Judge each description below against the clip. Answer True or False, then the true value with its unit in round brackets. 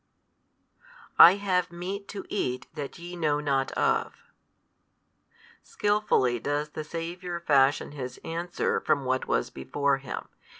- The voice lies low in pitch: False (155 Hz)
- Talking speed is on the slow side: True (125 wpm)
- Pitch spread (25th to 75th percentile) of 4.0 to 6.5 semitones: True (4.4 semitones)